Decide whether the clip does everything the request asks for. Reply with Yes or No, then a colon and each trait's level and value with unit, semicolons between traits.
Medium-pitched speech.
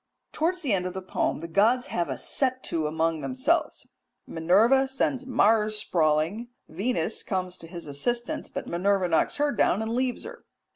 No: high, 210 Hz